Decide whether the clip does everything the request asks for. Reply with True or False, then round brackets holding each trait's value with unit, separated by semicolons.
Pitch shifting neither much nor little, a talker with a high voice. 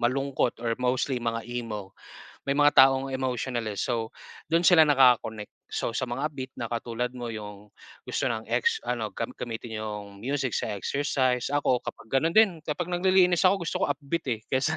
False (4.0 semitones; 130 Hz)